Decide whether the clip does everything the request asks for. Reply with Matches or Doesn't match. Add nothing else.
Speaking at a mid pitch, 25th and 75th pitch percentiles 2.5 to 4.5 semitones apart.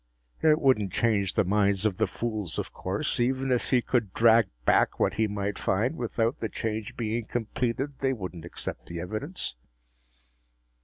Doesn't match